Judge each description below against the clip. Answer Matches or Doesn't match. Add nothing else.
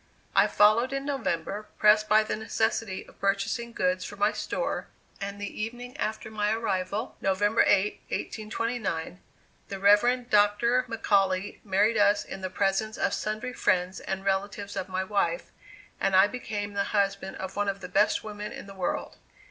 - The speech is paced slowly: Doesn't match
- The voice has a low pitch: Doesn't match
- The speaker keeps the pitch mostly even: Matches